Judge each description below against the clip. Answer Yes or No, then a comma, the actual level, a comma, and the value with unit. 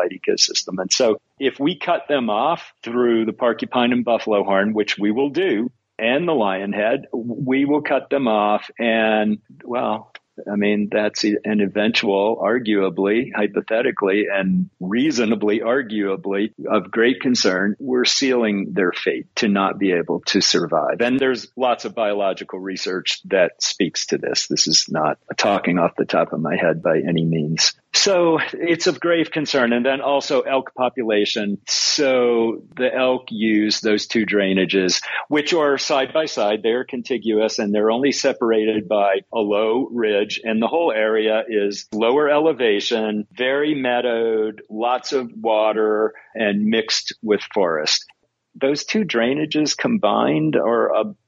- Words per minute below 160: Yes, average, 150 wpm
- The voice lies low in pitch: Yes, low, 110 Hz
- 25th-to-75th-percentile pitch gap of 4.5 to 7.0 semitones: No, average, 4.1 semitones